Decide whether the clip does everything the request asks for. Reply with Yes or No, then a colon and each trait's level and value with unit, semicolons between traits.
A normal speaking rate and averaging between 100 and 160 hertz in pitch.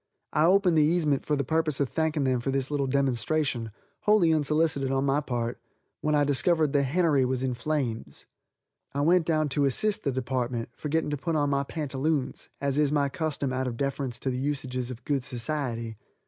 Yes: average, 195 wpm; medium, 140 Hz